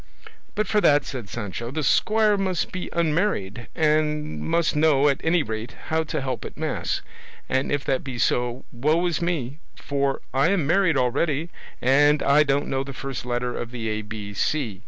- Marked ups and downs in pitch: No, average, 4.6 semitones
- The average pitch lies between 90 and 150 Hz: Yes, medium, 140 Hz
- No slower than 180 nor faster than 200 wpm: Yes, average, 185 wpm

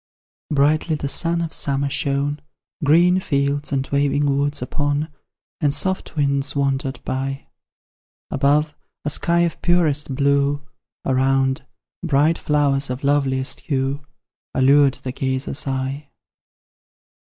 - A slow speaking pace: Yes, slow, 115 wpm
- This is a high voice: No, medium, 140 Hz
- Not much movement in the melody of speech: Yes, narrow, 1.6 semitones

